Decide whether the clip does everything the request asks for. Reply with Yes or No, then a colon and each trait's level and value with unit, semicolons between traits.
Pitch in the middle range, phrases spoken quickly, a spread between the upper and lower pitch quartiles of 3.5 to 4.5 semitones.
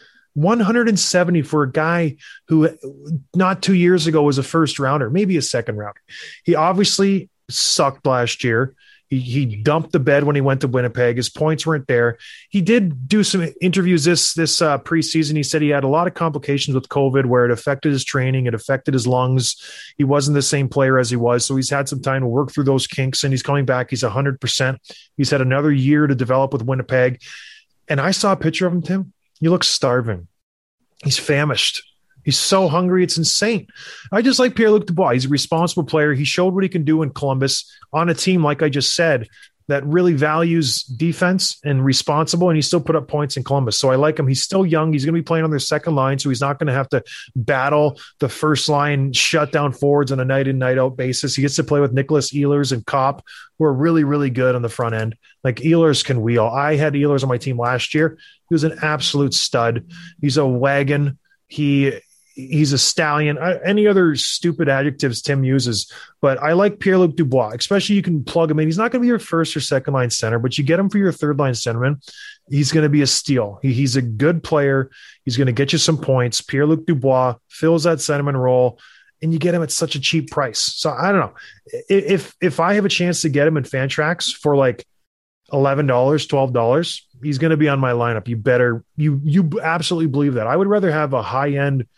Yes: medium, 145 Hz; fast, 225 wpm; average, 3.8 semitones